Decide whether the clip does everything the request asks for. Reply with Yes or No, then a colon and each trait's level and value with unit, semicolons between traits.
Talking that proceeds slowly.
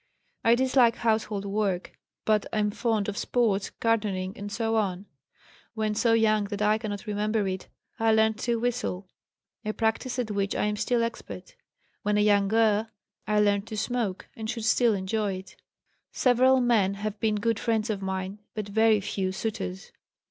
No: average, 165 wpm